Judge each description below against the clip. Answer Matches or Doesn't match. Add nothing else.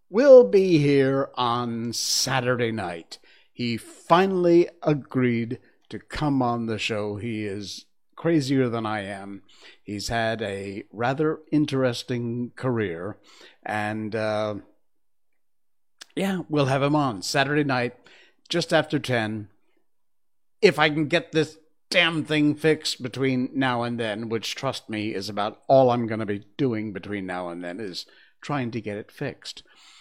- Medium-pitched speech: Doesn't match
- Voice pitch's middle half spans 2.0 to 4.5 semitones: Doesn't match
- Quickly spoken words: Doesn't match